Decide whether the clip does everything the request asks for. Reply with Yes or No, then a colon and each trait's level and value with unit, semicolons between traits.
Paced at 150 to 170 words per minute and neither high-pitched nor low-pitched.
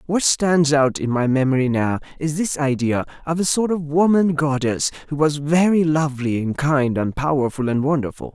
No: average, 185 wpm; medium, 145 Hz